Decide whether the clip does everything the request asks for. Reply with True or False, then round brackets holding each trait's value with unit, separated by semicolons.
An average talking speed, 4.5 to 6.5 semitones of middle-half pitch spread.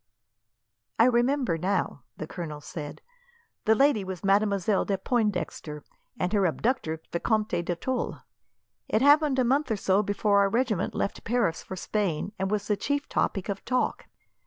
True (160 wpm; 4.8 semitones)